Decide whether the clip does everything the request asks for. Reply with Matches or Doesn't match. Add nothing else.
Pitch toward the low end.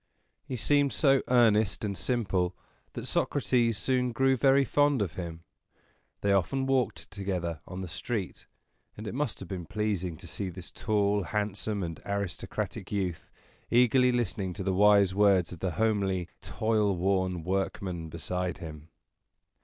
Matches